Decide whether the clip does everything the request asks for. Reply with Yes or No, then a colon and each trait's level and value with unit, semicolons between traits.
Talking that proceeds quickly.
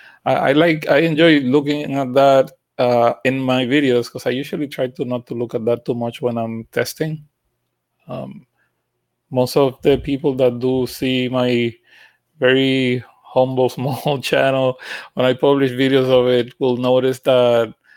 No: average, 160 wpm